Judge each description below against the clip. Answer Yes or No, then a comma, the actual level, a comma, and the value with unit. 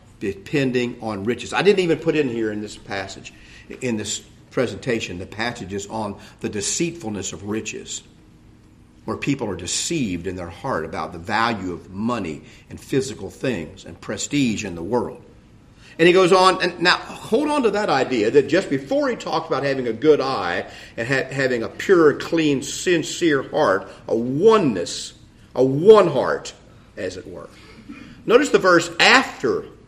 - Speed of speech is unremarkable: Yes, average, 165 wpm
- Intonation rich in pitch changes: Yes, wide, 8.9 semitones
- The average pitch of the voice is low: Yes, low, 120 Hz